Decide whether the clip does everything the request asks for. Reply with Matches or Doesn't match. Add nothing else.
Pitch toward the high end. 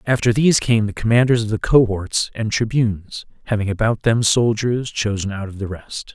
Doesn't match